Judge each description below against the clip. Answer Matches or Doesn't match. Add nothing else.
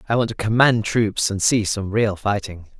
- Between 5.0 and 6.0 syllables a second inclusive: Doesn't match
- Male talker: Matches